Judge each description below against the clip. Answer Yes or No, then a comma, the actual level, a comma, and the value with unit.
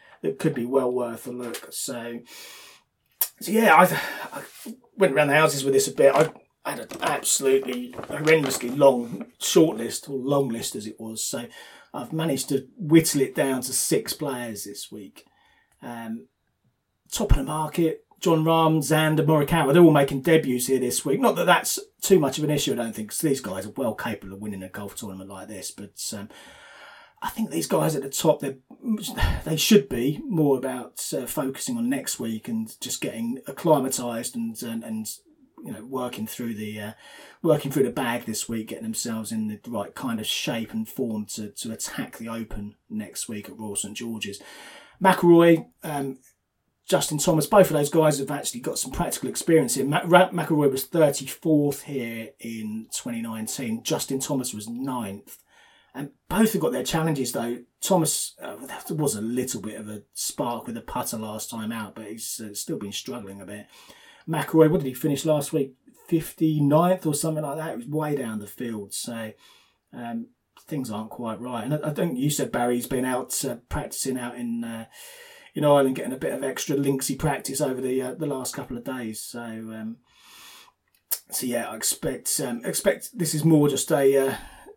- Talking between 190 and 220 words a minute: Yes, average, 195 wpm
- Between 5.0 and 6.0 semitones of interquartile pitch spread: Yes, wide, 5.5 semitones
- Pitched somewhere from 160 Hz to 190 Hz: No, low, 135 Hz